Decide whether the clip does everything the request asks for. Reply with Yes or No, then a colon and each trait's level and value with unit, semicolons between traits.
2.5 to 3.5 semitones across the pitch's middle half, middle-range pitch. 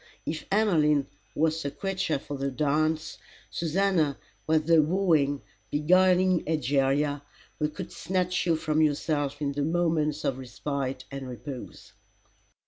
Yes: average, 2.9 semitones; medium, 155 Hz